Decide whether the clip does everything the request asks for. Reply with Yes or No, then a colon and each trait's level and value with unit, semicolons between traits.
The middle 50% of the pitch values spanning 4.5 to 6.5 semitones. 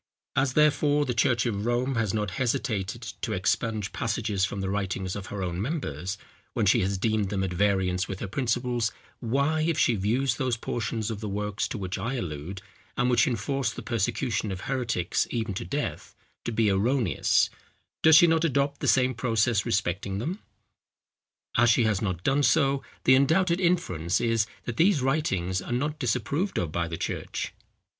Yes: wide, 5.4 semitones